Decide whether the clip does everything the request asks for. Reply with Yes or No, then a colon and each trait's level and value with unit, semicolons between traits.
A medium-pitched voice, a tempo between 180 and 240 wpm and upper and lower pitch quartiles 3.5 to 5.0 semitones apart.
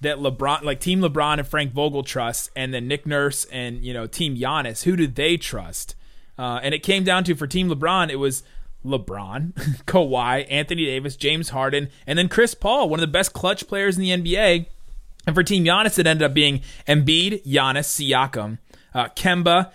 Yes: medium, 145 Hz; average, 195 wpm; average, 4.7 semitones